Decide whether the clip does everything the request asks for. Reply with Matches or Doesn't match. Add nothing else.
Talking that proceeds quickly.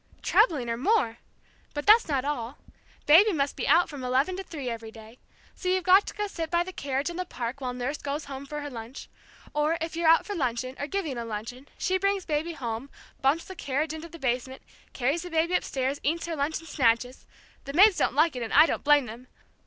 Matches